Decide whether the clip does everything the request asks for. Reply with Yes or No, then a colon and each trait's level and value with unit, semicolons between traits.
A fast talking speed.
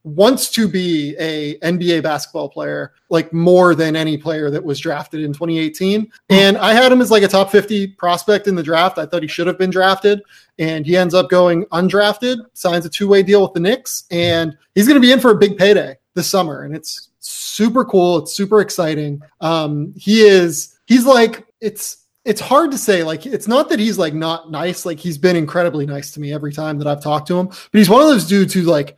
Yes: fast, 225 wpm